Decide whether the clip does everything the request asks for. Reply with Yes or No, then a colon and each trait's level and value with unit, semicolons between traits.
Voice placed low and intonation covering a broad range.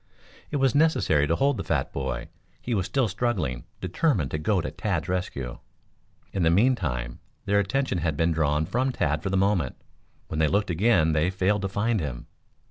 Yes: very low, 90 Hz; wide, 5.8 semitones